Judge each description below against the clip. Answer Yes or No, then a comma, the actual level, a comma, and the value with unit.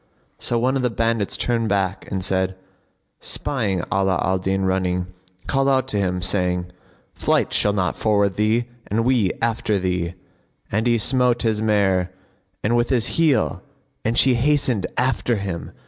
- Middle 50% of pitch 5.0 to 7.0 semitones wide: No, average, 4.1 semitones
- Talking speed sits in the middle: Yes, average, 150 wpm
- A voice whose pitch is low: Yes, low, 105 Hz